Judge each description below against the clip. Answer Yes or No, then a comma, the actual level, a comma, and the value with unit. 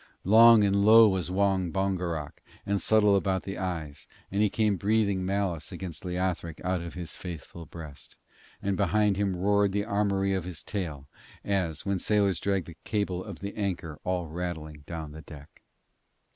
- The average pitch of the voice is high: No, very low, 95 Hz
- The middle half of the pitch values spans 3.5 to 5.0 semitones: No, average, 2.9 semitones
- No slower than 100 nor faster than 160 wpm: No, average, 170 wpm